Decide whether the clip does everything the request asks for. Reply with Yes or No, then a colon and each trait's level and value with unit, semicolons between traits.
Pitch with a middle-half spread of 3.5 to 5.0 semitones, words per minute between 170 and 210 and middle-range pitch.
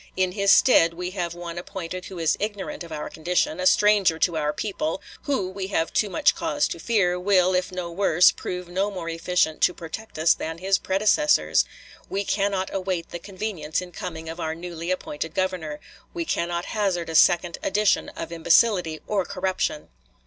No: average, 2.8 semitones; average, 185 wpm; medium, 180 Hz